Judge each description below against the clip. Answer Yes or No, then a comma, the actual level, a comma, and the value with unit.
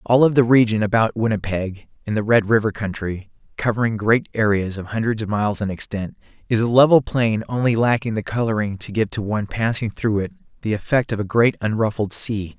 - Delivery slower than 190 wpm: No, average, 200 wpm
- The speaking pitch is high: No, low, 110 Hz